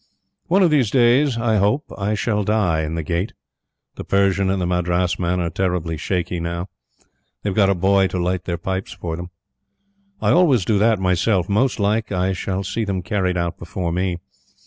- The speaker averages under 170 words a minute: No, average, 190 wpm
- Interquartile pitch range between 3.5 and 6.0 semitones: No, average, 3.1 semitones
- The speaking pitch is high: No, very low, 95 Hz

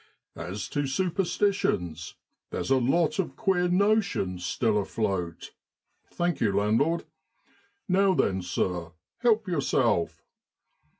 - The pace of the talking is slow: Yes, slow, 110 wpm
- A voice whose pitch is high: No, low, 135 Hz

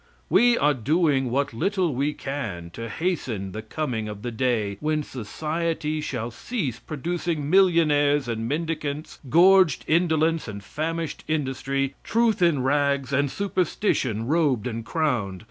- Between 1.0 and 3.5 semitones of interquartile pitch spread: No, average, 5.2 semitones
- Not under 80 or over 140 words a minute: Yes, slow, 135 wpm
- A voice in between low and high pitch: Yes, medium, 145 Hz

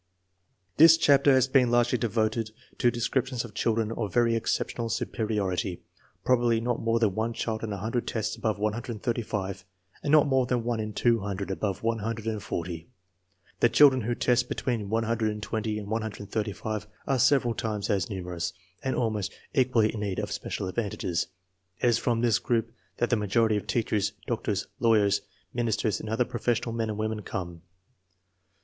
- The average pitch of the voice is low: Yes, low, 110 Hz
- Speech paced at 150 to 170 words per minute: Yes, average, 165 wpm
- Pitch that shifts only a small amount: Yes, narrow, 2.3 semitones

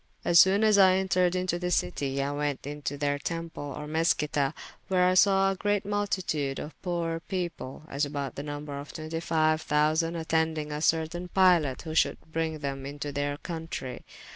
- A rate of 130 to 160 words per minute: No, average, 175 wpm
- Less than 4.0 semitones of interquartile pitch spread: Yes, average, 3.6 semitones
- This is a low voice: No, medium, 160 Hz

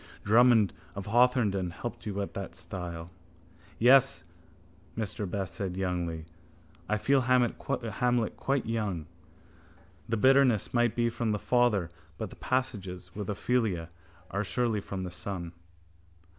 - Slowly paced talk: Yes, slow, 130 wpm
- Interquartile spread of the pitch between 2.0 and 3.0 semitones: No, average, 4.5 semitones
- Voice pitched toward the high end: No, low, 105 Hz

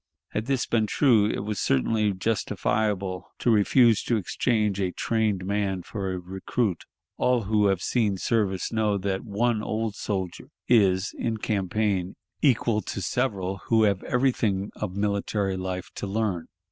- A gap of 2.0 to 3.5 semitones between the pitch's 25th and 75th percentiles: Yes, narrow, 2.6 semitones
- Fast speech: No, average, 150 wpm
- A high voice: No, low, 105 Hz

